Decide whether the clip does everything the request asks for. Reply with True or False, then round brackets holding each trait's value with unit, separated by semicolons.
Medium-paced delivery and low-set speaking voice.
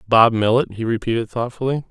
True (160 wpm; 115 Hz)